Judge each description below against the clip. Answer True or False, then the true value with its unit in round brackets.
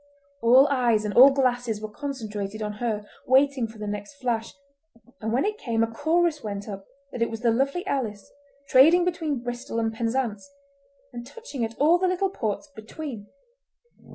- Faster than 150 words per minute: True (175 wpm)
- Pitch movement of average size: True (4.4 semitones)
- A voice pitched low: False (240 Hz)